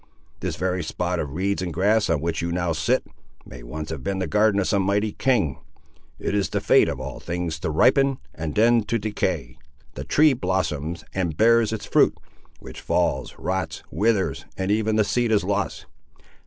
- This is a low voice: Yes, very low, 95 Hz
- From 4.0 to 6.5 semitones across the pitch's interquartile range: Yes, average, 4.8 semitones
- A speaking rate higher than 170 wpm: Yes, average, 190 wpm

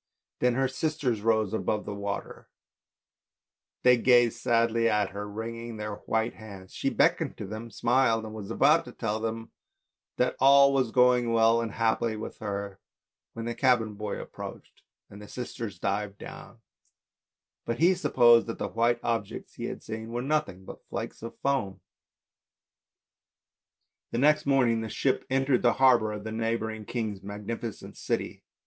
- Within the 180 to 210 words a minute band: No, average, 160 wpm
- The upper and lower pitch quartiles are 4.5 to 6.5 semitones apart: No, narrow, 2.4 semitones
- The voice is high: No, low, 115 Hz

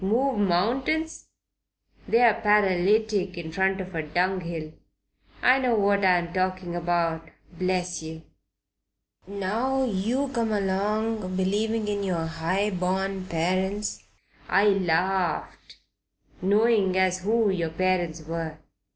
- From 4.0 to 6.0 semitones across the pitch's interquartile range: No, average, 3.0 semitones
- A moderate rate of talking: No, slow, 110 wpm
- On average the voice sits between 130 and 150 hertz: No, high, 190 Hz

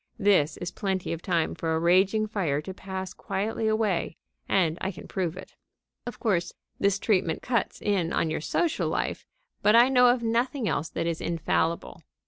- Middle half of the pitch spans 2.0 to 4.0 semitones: No, average, 4.4 semitones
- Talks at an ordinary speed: Yes, average, 180 wpm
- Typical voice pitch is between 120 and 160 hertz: No, high, 190 Hz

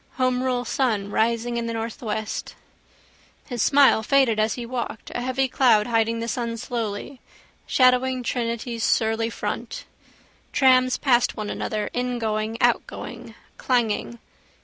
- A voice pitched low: No, high, 235 Hz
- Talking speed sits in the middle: No, slow, 125 wpm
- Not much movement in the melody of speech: Yes, narrow, 2.2 semitones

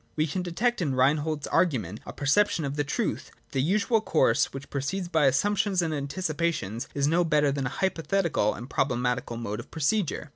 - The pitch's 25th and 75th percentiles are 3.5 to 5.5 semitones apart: Yes, average, 4.6 semitones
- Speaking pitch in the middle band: Yes, medium, 150 Hz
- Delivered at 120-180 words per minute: No, fast, 205 wpm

